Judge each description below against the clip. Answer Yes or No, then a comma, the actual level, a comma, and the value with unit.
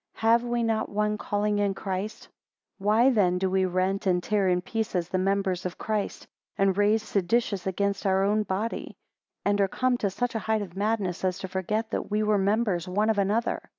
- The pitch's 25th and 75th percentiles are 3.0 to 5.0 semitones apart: No, narrow, 2.4 semitones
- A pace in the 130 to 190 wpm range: No, fast, 205 wpm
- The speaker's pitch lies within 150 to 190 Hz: No, high, 200 Hz